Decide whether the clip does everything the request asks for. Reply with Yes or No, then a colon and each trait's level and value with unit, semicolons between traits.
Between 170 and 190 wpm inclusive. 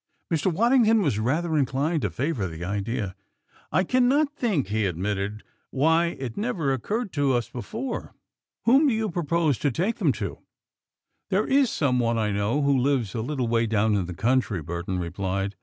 Yes: average, 175 wpm